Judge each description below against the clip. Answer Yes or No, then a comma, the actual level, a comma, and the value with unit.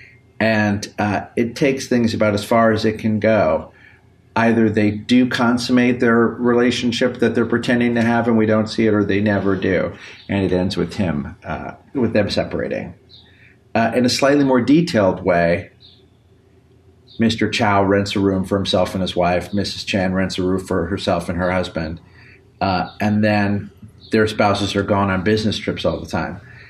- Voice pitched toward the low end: Yes, low, 105 Hz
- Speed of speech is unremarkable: Yes, average, 180 wpm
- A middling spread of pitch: Yes, average, 3.4 semitones